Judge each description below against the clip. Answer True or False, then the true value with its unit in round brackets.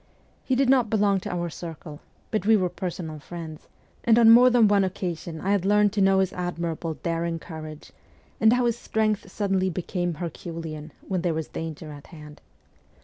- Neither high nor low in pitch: True (180 Hz)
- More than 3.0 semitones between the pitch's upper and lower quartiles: True (4.1 semitones)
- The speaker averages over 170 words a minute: True (185 wpm)